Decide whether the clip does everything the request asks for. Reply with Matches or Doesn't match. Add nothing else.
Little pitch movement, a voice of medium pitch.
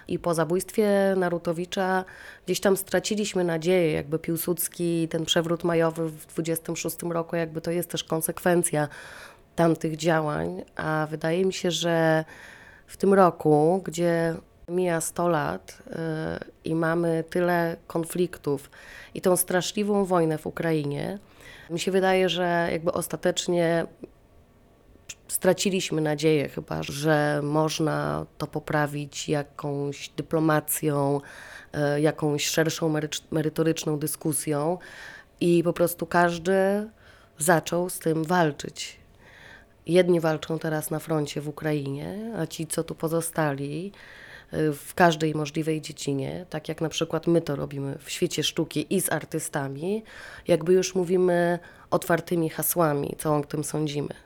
Matches